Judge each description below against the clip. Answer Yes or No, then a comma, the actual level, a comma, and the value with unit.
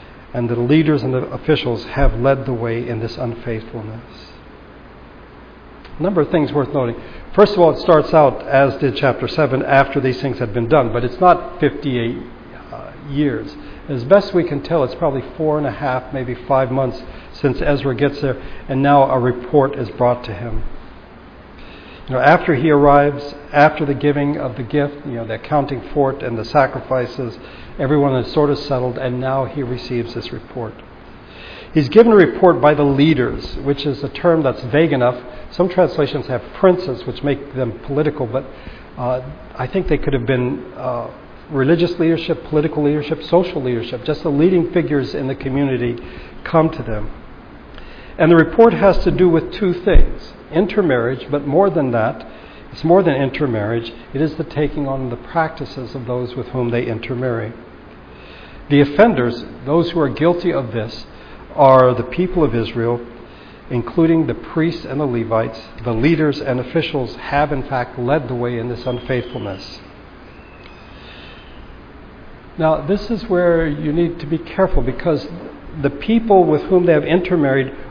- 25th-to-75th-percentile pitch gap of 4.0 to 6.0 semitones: Yes, average, 4.3 semitones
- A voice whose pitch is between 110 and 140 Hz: Yes, low, 135 Hz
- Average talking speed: Yes, average, 170 wpm